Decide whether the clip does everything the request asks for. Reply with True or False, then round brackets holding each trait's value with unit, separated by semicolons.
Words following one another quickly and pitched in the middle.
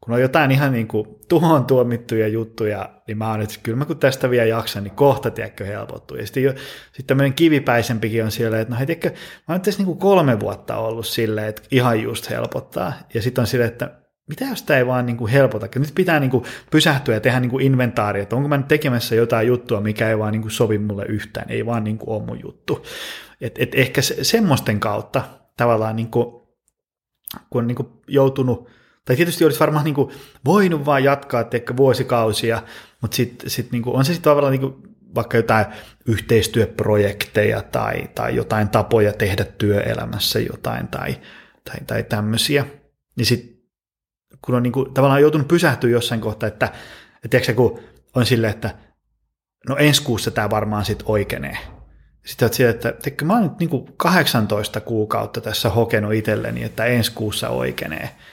False (185 wpm; 120 Hz)